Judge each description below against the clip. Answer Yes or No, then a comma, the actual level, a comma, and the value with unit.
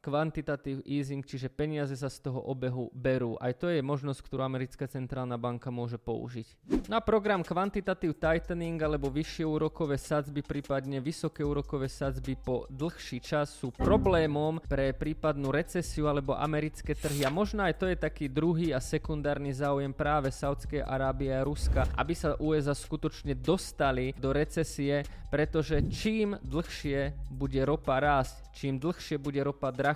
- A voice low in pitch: No, medium, 145 Hz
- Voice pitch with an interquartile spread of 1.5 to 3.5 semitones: Yes, narrow, 2.6 semitones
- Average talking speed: Yes, average, 150 wpm